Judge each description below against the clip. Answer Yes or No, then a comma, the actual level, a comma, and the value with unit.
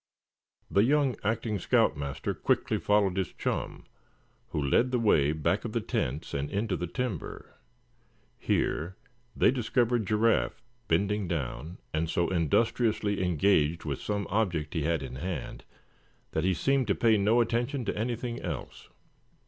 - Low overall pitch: Yes, low, 100 Hz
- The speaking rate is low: No, average, 150 wpm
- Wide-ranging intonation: Yes, wide, 6.1 semitones